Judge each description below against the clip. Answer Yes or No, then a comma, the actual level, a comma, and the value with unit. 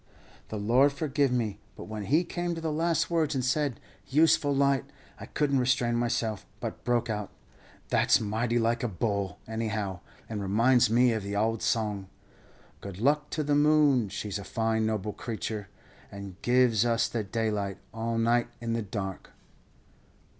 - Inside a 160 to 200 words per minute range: Yes, average, 165 wpm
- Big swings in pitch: No, average, 4.3 semitones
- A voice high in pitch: No, low, 115 Hz